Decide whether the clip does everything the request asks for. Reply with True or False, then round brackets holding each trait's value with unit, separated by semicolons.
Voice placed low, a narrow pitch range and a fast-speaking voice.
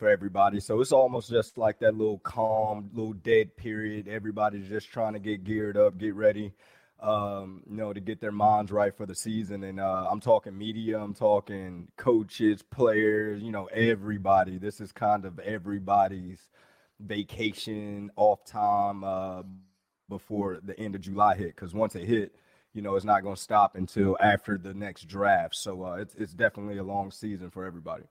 False (105 Hz; 1.7 semitones; 185 wpm)